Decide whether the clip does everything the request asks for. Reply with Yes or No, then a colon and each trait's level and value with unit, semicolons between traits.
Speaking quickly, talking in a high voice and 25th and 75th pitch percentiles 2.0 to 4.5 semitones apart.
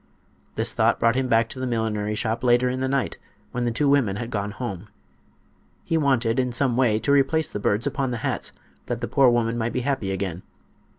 No: fast, 220 wpm; low, 120 Hz; average, 3.0 semitones